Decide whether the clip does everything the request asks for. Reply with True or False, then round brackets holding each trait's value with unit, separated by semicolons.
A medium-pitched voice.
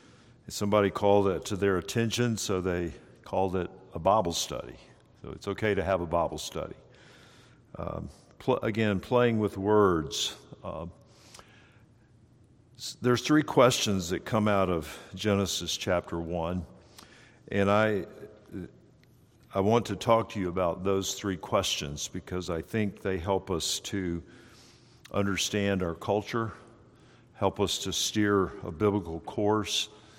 False (100 Hz)